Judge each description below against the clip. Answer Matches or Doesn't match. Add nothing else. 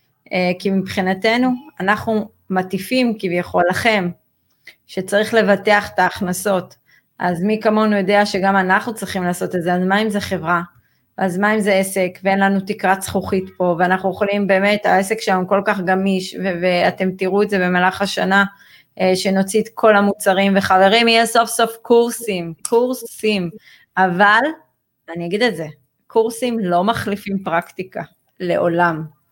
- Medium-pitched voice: Doesn't match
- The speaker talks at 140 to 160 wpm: Matches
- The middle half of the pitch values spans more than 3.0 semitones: Doesn't match